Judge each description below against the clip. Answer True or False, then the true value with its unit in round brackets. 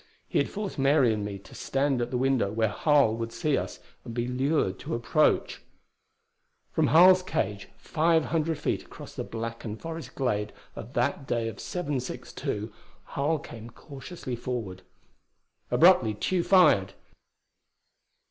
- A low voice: True (125 Hz)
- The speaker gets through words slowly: False (145 wpm)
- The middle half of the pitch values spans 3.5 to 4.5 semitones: False (5.5 semitones)